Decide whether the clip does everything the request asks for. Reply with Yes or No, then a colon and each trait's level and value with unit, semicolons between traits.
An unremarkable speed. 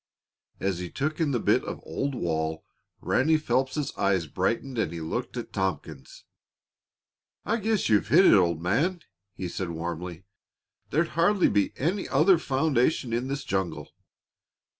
Yes: average, 150 wpm